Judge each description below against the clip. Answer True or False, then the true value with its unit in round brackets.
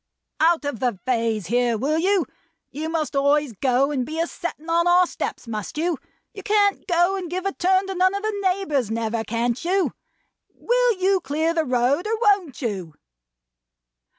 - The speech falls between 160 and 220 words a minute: True (180 wpm)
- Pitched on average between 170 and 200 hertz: False (320 Hz)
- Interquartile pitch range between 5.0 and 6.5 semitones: False (7.1 semitones)